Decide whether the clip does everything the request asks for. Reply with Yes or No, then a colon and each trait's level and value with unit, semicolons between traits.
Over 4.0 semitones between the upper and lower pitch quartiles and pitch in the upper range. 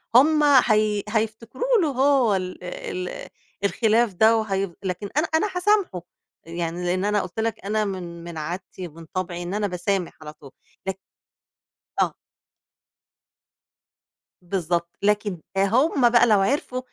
Yes: average, 4.6 semitones; high, 200 Hz